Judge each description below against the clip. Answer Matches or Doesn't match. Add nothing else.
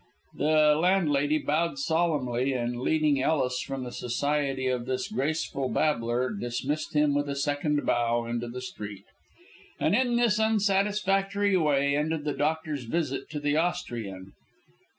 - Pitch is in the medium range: Matches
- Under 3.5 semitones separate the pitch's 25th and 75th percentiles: Doesn't match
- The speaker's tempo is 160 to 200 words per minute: Doesn't match